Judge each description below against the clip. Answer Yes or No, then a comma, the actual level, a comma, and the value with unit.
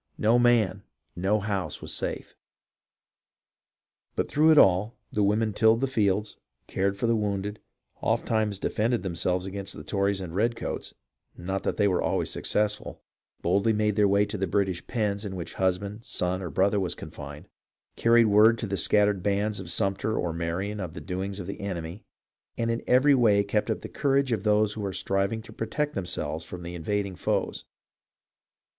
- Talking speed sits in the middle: Yes, average, 180 wpm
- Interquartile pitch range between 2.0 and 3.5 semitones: Yes, narrow, 2.6 semitones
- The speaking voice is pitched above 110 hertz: No, low, 100 Hz